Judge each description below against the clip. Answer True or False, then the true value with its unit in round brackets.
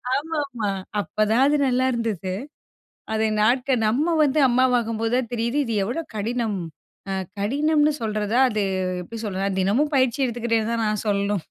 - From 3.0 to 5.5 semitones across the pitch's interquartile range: True (3.5 semitones)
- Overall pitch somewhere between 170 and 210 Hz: False (230 Hz)